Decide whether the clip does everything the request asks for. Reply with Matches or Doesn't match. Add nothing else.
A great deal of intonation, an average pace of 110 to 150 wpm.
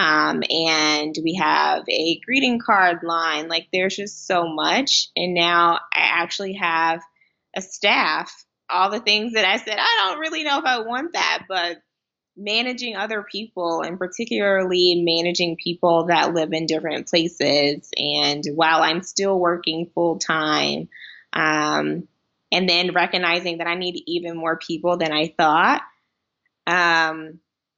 Doesn't match